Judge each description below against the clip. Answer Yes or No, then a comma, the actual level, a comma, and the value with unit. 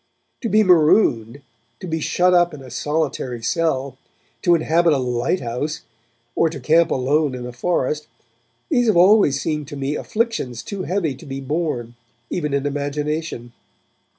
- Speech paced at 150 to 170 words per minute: Yes, average, 155 wpm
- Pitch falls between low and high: Yes, medium, 150 Hz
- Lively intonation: No, average, 4.5 semitones